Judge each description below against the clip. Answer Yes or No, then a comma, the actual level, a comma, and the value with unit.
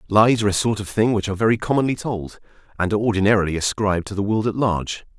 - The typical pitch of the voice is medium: No, low, 105 Hz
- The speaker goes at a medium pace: No, fast, 230 wpm